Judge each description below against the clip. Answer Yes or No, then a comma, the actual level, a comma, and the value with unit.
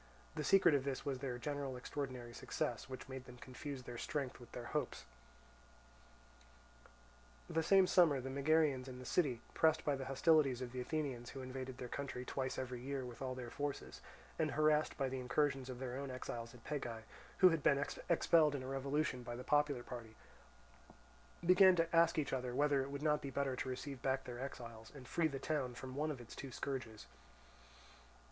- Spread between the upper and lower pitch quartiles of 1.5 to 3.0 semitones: Yes, narrow, 2.6 semitones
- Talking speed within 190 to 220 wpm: Yes, average, 195 wpm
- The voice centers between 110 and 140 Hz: Yes, low, 135 Hz